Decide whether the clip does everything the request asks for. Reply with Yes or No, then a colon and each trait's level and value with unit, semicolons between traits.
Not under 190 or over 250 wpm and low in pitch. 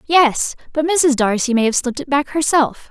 No: fast, 205 wpm; very high, 280 Hz